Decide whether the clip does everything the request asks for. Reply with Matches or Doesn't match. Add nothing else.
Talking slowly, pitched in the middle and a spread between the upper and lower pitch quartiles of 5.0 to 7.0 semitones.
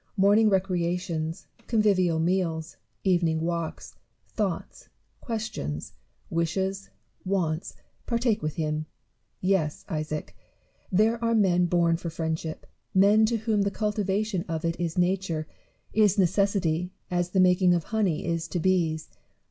Doesn't match